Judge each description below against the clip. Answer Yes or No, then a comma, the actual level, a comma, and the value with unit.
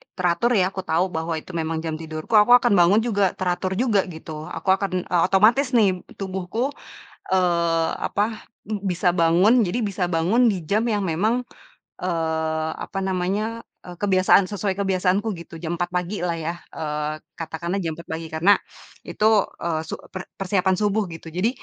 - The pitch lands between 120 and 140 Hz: No, medium, 185 Hz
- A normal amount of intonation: Yes, average, 3.6 semitones